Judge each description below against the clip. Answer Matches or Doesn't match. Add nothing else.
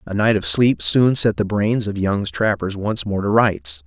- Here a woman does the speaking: Doesn't match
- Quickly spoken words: Matches